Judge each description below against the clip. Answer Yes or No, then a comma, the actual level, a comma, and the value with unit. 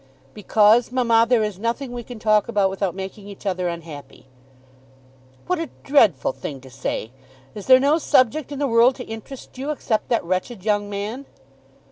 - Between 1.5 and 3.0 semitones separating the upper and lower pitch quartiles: No, average, 4.7 semitones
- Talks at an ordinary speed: Yes, average, 175 wpm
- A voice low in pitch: No, high, 220 Hz